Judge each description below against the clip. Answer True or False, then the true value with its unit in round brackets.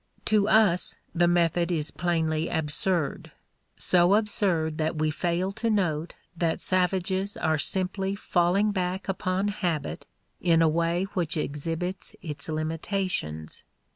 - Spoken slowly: True (125 wpm)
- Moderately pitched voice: True (175 Hz)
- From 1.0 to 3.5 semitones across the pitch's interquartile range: True (3.0 semitones)